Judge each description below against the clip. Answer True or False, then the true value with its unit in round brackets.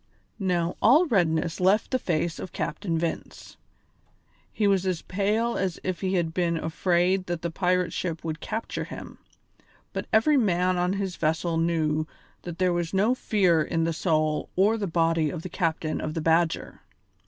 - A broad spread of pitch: False (2.8 semitones)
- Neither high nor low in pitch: True (175 Hz)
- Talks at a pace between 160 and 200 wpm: True (175 wpm)